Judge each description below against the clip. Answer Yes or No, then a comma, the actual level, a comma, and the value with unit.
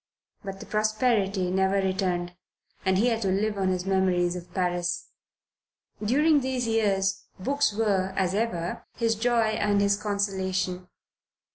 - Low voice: No, high, 195 Hz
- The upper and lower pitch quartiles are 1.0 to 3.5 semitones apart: Yes, average, 2.7 semitones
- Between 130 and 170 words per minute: Yes, average, 140 wpm